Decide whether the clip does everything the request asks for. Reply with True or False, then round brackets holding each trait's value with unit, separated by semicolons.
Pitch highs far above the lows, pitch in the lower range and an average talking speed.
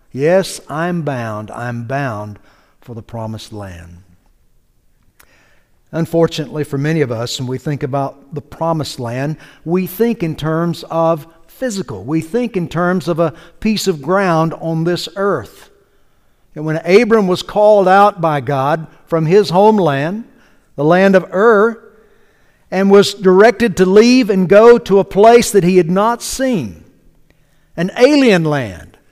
False (6.0 semitones; 165 Hz; 150 wpm)